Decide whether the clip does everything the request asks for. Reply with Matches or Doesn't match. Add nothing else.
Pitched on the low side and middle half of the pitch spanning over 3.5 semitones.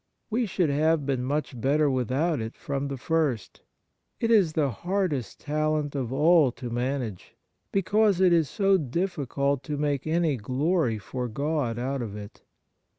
Doesn't match